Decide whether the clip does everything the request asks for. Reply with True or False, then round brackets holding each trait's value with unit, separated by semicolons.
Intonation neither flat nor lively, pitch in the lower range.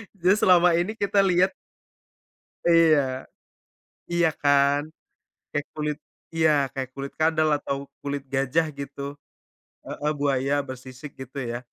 False (3.0 semitones; 145 Hz)